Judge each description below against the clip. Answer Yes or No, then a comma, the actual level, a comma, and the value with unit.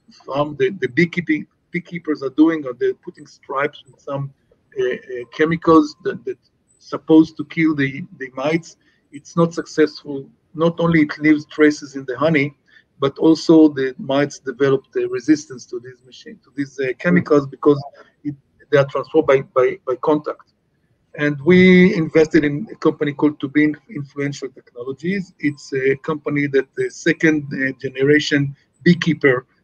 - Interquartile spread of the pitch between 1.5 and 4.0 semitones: Yes, average, 3.1 semitones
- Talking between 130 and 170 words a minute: Yes, average, 155 wpm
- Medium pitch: Yes, medium, 150 Hz